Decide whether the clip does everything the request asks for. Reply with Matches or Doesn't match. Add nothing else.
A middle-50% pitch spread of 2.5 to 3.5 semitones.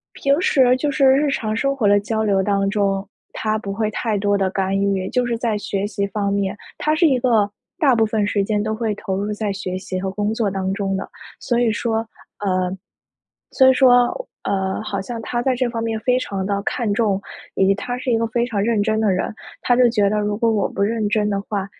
Matches